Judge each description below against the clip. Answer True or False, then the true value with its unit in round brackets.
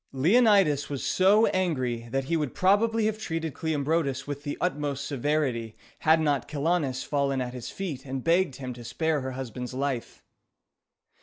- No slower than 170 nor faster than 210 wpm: False (160 wpm)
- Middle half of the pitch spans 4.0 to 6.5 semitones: True (4.3 semitones)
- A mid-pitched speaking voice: True (145 Hz)